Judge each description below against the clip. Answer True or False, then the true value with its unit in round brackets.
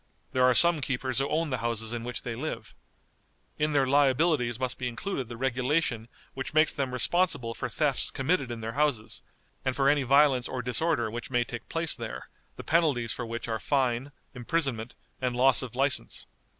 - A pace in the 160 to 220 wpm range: True (190 wpm)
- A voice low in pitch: True (130 Hz)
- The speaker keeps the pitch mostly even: False (3.4 semitones)